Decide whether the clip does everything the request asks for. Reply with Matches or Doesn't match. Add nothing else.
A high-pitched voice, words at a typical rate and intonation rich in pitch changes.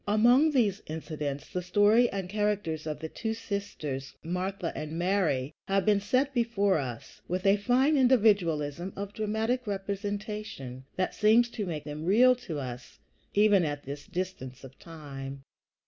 Matches